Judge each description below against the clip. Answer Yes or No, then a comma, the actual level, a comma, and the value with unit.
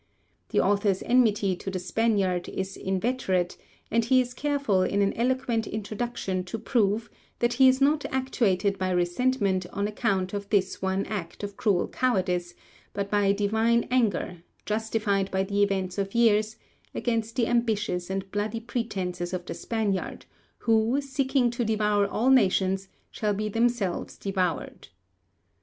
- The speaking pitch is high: Yes, high, 205 Hz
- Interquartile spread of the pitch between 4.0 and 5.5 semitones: No, average, 3.6 semitones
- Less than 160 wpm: Yes, average, 150 wpm